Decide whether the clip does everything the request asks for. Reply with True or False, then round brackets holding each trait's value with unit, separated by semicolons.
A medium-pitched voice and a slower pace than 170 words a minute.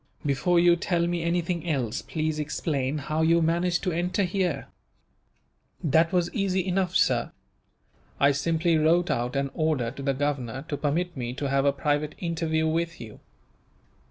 True (160 Hz; 160 wpm)